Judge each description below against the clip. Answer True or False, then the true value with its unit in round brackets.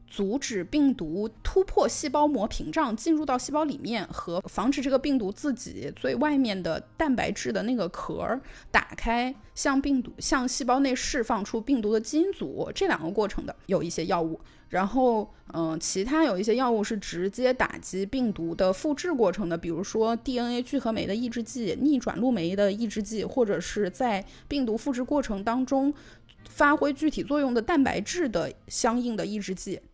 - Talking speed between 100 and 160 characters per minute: False (285 characters per minute)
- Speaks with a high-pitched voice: True (240 Hz)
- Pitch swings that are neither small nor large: False (5.7 semitones)